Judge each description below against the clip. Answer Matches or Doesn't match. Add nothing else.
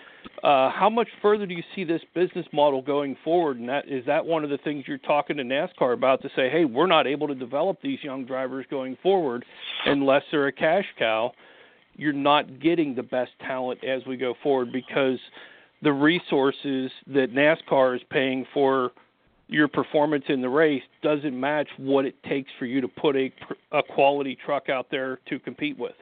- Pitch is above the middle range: Doesn't match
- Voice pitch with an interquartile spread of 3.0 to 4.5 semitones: Doesn't match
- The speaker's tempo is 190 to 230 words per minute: Matches